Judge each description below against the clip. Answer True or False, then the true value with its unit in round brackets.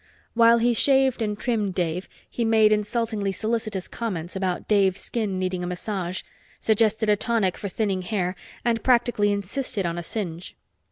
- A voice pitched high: True (210 Hz)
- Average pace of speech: True (160 wpm)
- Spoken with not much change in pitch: False (3.6 semitones)